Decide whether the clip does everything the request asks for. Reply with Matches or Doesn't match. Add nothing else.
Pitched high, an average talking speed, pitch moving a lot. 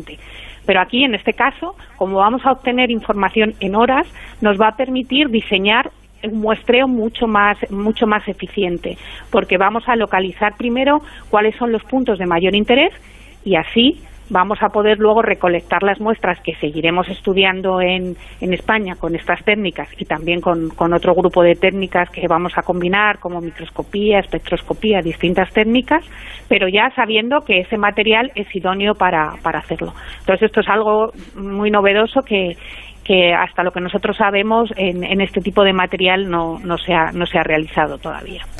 Doesn't match